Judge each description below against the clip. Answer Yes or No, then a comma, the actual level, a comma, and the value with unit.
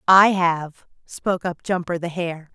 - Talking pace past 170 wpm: No, average, 165 wpm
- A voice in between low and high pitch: Yes, medium, 175 Hz